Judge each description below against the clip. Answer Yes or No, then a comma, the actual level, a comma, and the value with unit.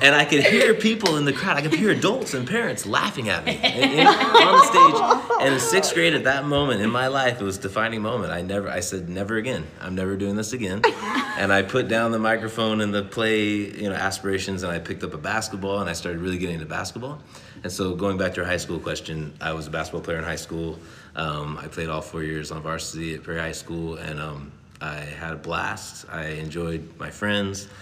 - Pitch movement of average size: Yes, average, 5.0 semitones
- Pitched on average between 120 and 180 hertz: No, very low, 95 Hz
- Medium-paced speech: No, fast, 235 wpm